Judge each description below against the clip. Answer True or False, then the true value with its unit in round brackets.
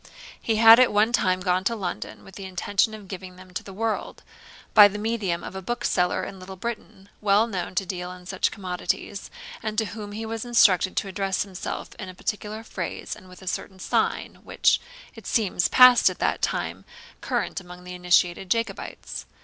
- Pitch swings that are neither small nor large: True (3.0 semitones)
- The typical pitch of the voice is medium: False (195 Hz)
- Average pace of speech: True (195 wpm)